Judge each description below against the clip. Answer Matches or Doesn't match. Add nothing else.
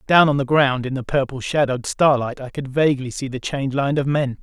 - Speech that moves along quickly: Matches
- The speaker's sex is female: Doesn't match